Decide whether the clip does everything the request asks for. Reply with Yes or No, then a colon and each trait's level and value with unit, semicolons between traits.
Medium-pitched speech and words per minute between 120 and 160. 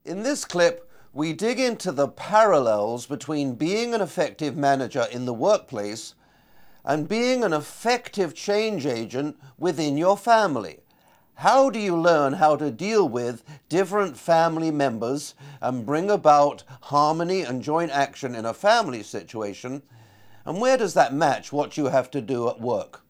Yes: medium, 150 Hz; average, 155 wpm